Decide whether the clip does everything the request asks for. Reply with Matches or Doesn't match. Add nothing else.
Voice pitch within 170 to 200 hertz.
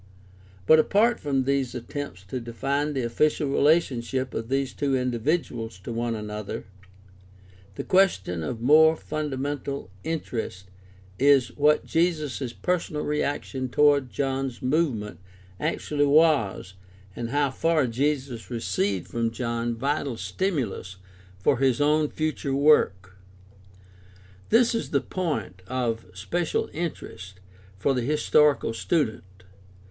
Doesn't match